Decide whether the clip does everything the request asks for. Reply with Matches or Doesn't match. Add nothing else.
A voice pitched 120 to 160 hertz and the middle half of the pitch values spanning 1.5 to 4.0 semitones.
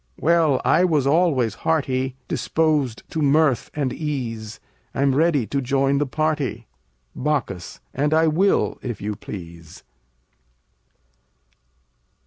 Matches